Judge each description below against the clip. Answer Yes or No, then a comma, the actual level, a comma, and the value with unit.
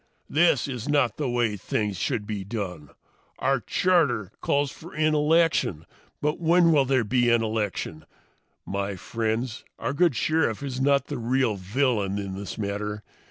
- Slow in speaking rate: No, average, 160 wpm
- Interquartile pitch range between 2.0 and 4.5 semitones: No, wide, 5.6 semitones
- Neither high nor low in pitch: No, low, 120 Hz